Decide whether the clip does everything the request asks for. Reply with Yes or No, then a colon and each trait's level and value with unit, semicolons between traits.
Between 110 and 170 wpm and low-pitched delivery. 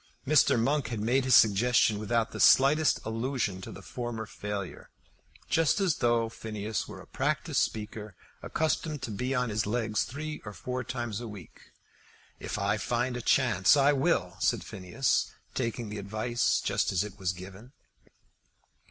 Yes: average, 160 wpm; low, 115 Hz